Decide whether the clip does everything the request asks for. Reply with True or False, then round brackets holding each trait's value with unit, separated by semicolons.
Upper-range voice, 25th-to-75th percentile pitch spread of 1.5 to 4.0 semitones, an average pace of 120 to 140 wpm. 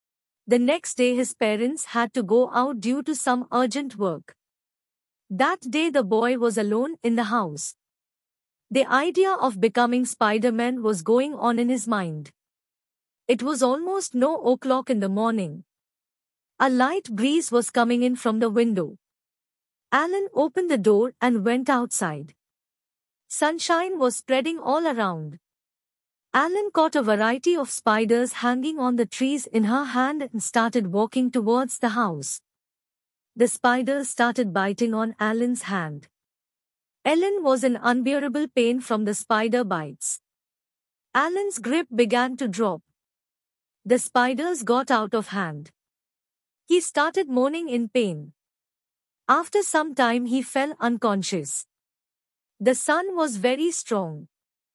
True (245 Hz; 3.7 semitones; 135 wpm)